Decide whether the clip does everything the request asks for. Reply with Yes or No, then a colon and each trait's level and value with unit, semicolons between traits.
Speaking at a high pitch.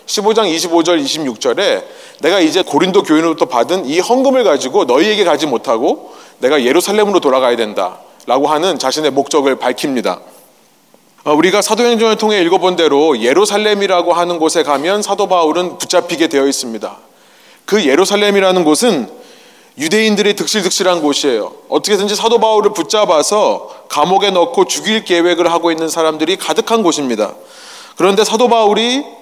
Yes: high, 200 Hz